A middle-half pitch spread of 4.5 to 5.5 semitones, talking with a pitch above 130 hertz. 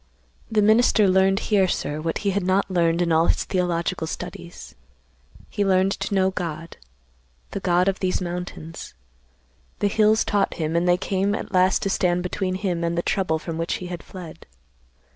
No: narrow, 2.4 semitones; medium, 185 Hz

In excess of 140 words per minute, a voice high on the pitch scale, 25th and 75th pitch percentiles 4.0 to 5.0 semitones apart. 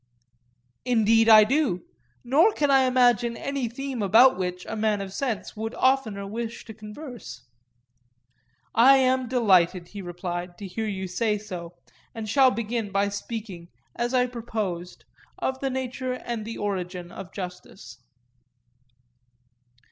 No: slow, 135 wpm; high, 220 Hz; average, 4.6 semitones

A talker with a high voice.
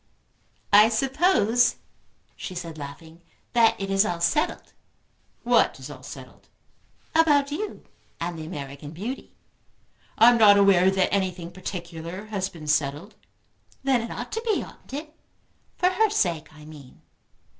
Yes: high, 195 Hz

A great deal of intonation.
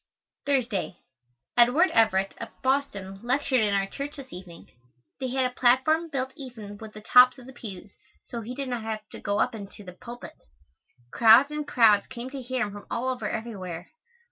No: average, 4.1 semitones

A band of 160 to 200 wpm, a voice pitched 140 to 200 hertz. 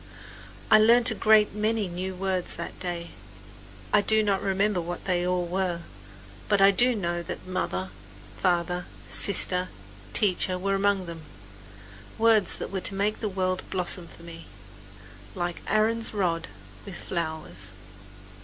No: average, 145 wpm; medium, 185 Hz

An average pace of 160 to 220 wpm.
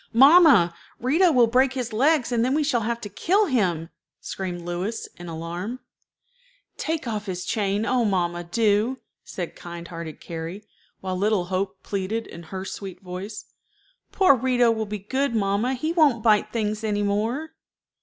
Yes: average, 165 wpm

